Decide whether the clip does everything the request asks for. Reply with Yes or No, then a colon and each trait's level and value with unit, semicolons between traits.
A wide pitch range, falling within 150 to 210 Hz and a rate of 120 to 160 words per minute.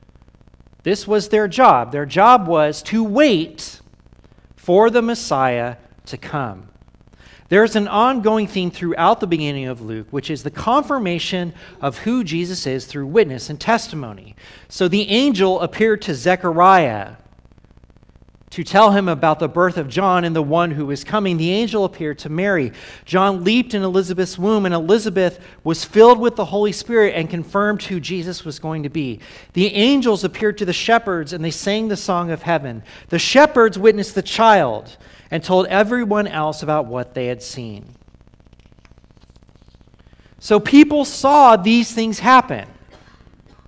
Yes: wide, 5.8 semitones; medium, 185 Hz; average, 155 wpm